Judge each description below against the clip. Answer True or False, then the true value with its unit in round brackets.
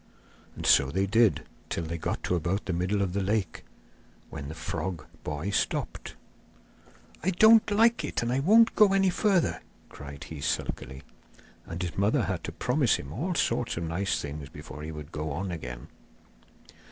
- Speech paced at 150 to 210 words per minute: True (175 wpm)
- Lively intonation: True (8.3 semitones)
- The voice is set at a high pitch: False (90 Hz)